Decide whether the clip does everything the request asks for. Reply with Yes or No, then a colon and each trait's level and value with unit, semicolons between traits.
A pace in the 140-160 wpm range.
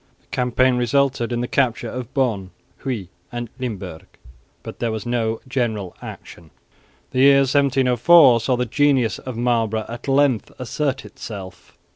Yes: average, 145 wpm